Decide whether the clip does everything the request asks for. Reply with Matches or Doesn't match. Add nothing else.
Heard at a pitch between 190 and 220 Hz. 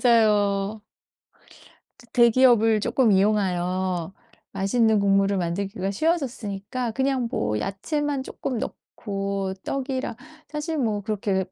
Matches